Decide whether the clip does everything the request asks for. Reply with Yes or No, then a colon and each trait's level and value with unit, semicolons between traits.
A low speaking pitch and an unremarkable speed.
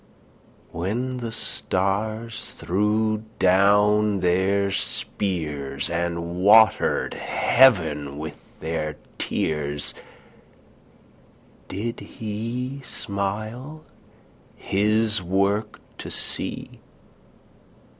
No: low, 100 Hz; slow, 65 wpm